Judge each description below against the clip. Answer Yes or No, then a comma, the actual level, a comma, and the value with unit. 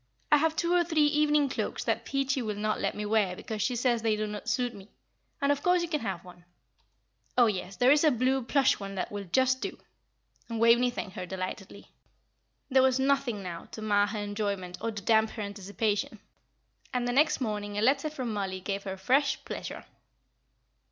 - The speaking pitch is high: Yes, high, 225 Hz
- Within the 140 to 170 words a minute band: No, fast, 205 wpm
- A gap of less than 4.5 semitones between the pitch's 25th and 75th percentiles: No, average, 4.8 semitones